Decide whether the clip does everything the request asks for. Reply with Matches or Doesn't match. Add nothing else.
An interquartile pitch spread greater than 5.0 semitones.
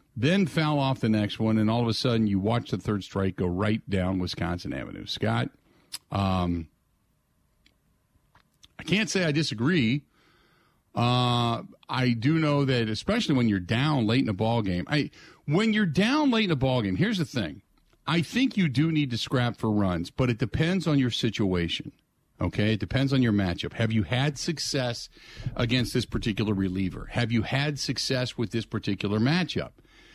Matches